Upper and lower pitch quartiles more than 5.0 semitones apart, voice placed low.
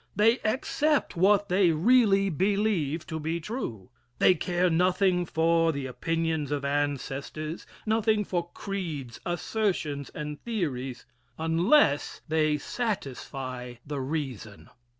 No: wide, 5.4 semitones; medium, 165 Hz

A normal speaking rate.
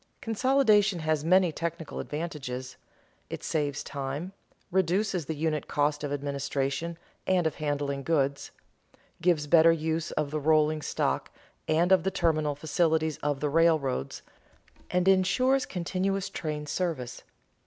No: slow, 130 wpm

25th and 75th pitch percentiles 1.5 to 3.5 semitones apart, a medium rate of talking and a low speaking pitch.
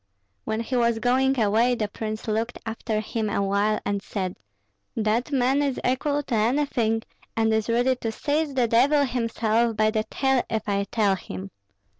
No: average, 2.8 semitones; average, 170 wpm; high, 225 Hz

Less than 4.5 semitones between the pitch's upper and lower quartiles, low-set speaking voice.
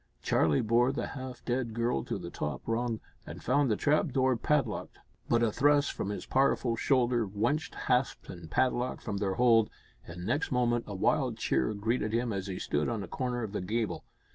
Yes: average, 3.7 semitones; low, 120 Hz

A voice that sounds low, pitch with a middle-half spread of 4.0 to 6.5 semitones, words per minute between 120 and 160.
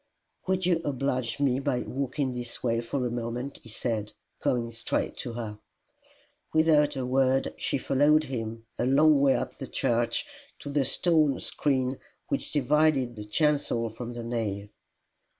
No: low, 130 Hz; average, 3.5 semitones; average, 155 wpm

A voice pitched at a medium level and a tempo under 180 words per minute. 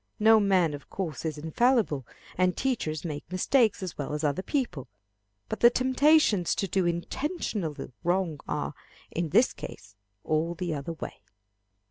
Yes: medium, 180 Hz; average, 150 wpm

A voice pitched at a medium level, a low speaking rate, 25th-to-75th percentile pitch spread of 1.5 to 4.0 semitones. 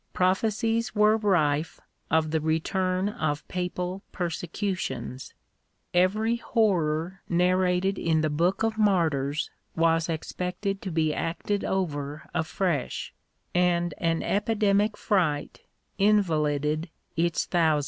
Yes: medium, 175 Hz; slow, 105 wpm; average, 3.7 semitones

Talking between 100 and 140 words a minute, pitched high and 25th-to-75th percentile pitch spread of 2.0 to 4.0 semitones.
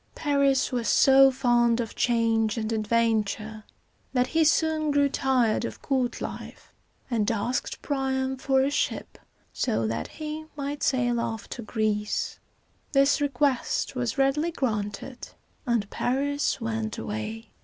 Yes: slow, 135 wpm; very high, 250 Hz; average, 3.6 semitones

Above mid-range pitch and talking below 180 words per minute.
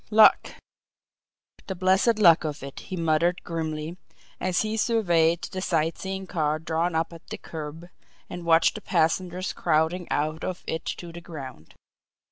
No: medium, 170 Hz; average, 155 wpm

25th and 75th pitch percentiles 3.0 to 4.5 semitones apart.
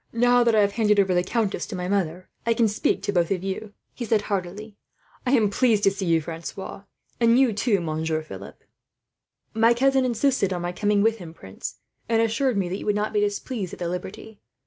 Yes: average, 4.0 semitones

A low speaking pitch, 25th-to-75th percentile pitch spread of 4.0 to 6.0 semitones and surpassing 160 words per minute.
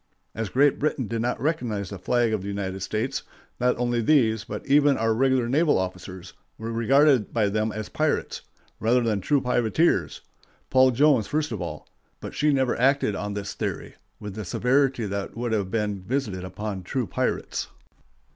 Yes: low, 115 Hz; average, 4.4 semitones; average, 175 wpm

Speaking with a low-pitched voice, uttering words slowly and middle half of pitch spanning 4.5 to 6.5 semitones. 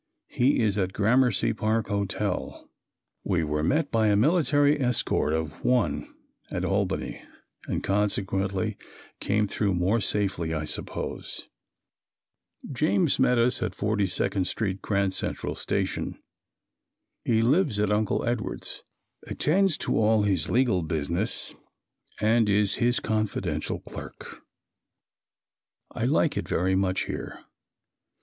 No: low, 105 Hz; slow, 120 wpm; average, 3.9 semitones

